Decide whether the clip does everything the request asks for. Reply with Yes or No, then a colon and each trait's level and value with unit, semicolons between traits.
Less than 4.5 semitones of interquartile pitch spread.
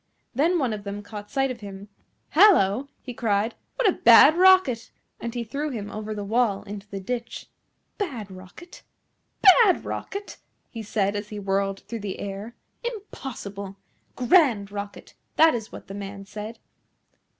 No: average, 5.0 semitones